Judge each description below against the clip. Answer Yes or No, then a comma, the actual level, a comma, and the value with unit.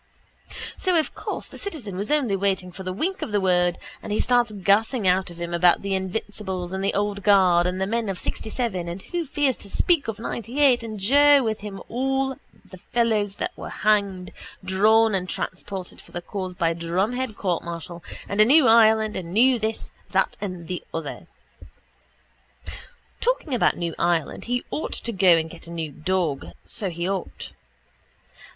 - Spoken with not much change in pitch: No, average, 4.2 semitones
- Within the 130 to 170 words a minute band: No, average, 185 wpm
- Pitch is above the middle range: Yes, high, 200 Hz